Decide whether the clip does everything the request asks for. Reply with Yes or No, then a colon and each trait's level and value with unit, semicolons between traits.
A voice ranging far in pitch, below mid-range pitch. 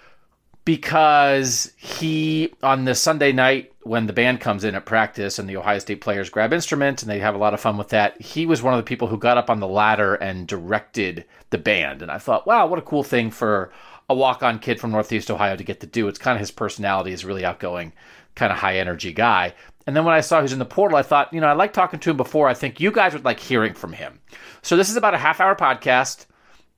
Yes: wide, 5.8 semitones; low, 120 Hz